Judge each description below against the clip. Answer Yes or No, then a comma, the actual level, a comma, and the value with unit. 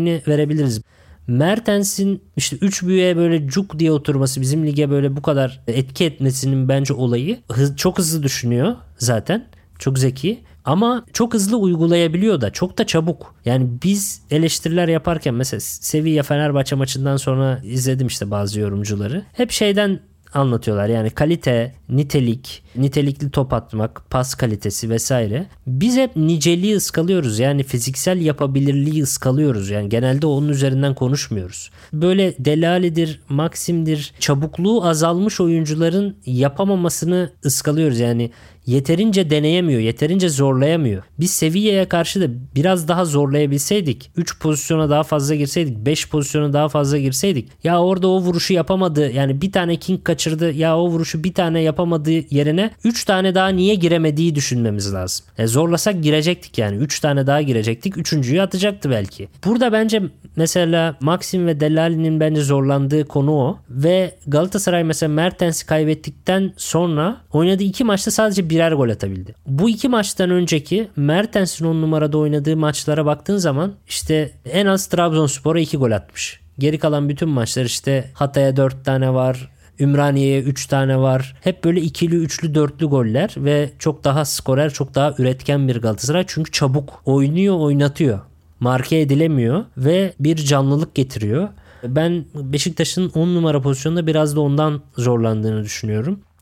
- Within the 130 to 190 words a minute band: Yes, fast, 140 wpm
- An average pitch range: Yes, average, 4.3 semitones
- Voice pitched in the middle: Yes, medium, 150 Hz